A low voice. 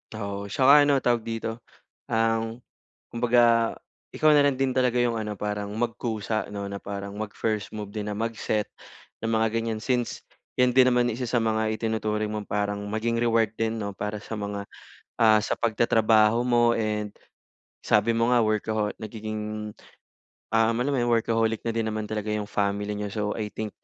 Yes: low, 110 Hz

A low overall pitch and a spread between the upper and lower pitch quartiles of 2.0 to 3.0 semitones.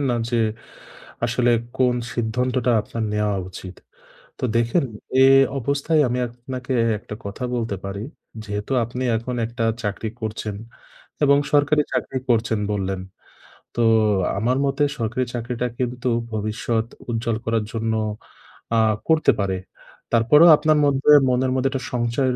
Yes: low, 120 Hz; narrow, 2.6 semitones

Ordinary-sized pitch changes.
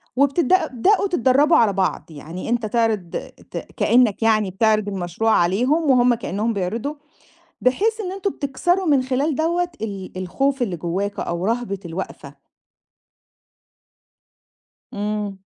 No: wide, 6.0 semitones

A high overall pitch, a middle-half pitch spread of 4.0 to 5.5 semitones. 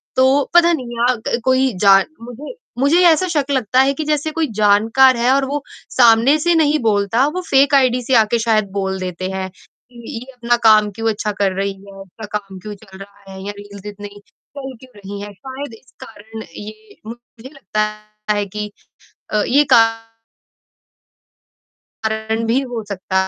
Yes: high, 225 Hz; average, 4.5 semitones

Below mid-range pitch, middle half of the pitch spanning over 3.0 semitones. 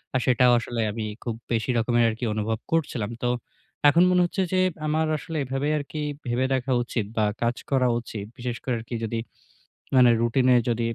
No: low, 120 Hz; average, 2.7 semitones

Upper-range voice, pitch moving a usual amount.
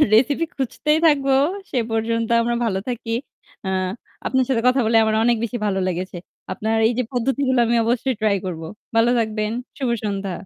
Yes: high, 230 Hz; average, 3.1 semitones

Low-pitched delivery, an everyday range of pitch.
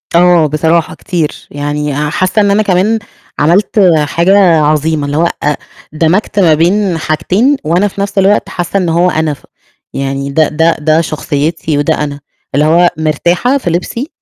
No: medium, 165 Hz; average, 3.6 semitones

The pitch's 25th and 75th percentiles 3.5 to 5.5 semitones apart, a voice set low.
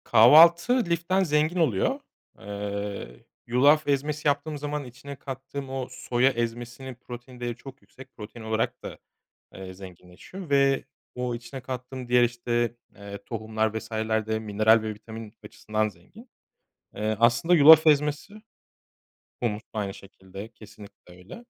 Yes: average, 4.6 semitones; low, 120 Hz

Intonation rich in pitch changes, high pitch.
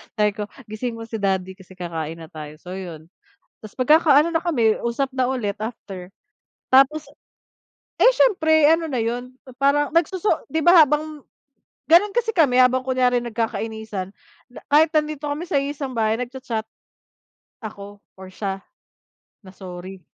Yes: wide, 6.7 semitones; high, 245 Hz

